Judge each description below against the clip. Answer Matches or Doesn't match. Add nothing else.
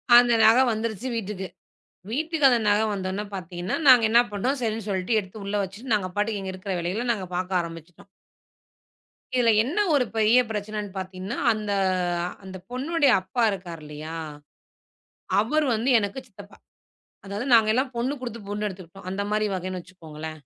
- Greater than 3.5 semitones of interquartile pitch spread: Matches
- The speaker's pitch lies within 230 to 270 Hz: Doesn't match